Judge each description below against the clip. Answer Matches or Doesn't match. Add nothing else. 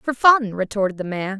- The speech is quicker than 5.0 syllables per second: Matches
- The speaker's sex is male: Doesn't match